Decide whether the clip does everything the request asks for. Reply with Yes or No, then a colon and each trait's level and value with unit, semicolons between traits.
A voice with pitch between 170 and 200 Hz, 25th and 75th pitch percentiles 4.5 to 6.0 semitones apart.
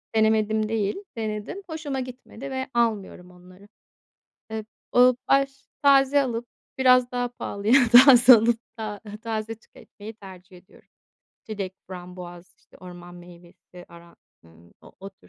No: high, 220 Hz; average, 5.2 semitones